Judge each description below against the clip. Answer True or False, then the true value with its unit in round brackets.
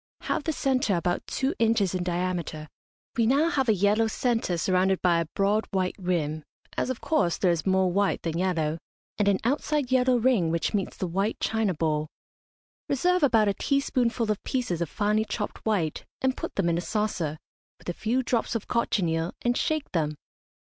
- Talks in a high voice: True (200 Hz)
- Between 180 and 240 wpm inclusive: True (190 wpm)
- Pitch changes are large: True (5.7 semitones)